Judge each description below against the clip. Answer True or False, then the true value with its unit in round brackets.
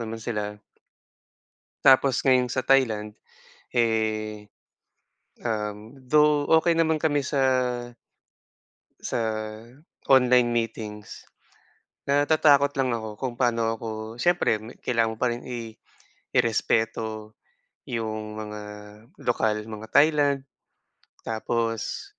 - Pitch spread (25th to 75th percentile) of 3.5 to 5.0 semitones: True (3.8 semitones)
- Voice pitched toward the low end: True (115 Hz)